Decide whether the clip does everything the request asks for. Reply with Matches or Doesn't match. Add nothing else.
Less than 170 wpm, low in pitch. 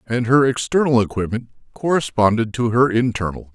Matches